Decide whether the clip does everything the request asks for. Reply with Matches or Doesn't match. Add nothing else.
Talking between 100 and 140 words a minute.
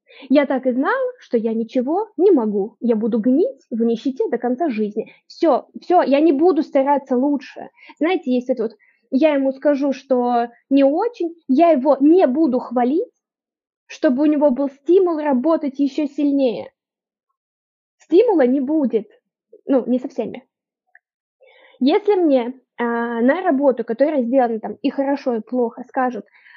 Doesn't match